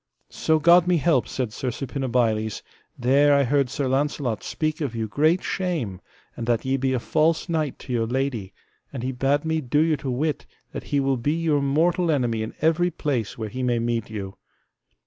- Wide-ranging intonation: No, average, 4.5 semitones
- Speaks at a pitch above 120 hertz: Yes, low, 135 Hz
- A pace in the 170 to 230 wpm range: Yes, average, 200 wpm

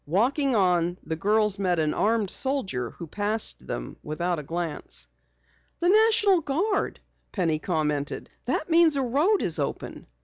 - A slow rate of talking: No, average, 145 wpm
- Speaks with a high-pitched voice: Yes, high, 200 Hz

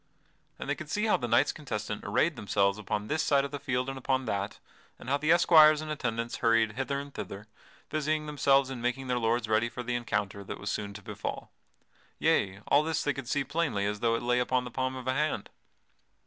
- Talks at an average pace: No, fast, 230 wpm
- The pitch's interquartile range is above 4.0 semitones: Yes, average, 4.5 semitones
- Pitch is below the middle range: Yes, low, 125 Hz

